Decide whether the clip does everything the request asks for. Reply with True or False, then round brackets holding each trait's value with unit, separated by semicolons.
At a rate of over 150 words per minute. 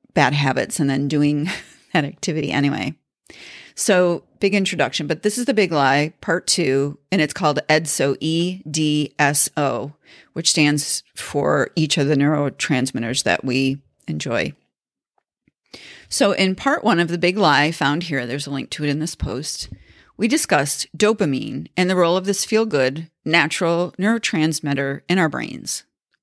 True (160 wpm)